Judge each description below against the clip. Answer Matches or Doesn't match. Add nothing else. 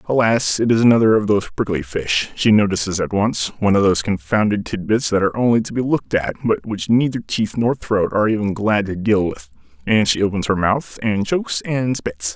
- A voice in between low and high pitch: Doesn't match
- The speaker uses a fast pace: Matches